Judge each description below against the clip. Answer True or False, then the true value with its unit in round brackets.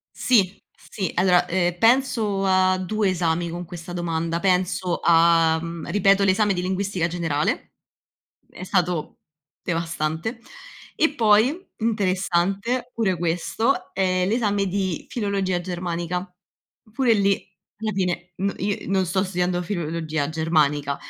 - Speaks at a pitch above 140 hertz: True (185 Hz)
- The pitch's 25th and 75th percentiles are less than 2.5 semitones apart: False (2.8 semitones)